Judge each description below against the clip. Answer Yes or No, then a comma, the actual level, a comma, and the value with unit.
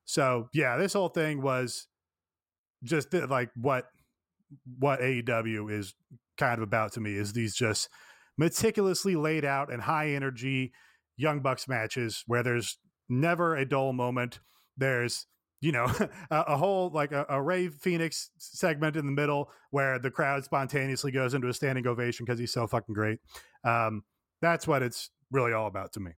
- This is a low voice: Yes, low, 130 Hz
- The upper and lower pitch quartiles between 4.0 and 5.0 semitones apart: Yes, average, 4.5 semitones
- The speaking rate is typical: Yes, average, 170 wpm